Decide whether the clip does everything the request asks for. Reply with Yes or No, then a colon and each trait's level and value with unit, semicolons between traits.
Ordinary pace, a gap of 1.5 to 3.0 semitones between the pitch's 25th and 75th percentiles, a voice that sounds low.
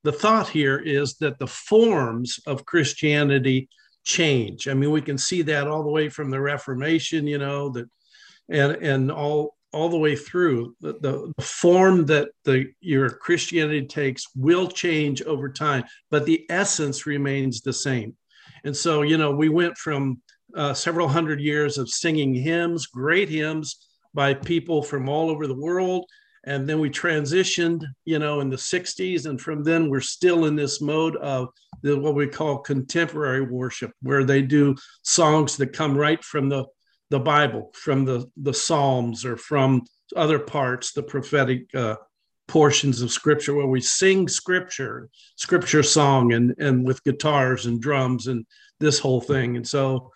No: average, 165 wpm; narrow, 2.6 semitones; medium, 145 Hz